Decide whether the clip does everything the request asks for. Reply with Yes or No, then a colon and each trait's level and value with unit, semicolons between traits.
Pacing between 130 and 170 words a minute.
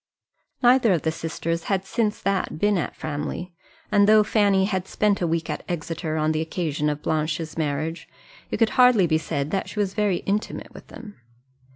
No: average, 190 wpm